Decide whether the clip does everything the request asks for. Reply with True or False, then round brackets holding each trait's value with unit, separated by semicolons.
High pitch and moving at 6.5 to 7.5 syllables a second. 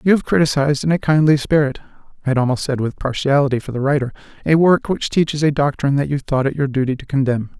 False (140 Hz; 6.8 syllables/s)